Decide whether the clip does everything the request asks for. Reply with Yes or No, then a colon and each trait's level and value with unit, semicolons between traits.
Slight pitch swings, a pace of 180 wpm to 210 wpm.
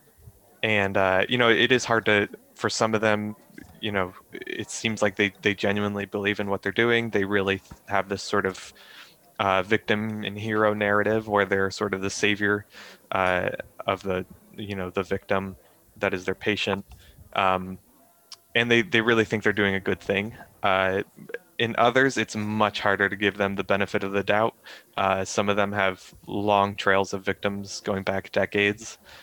Yes: narrow, 1.6 semitones; average, 185 wpm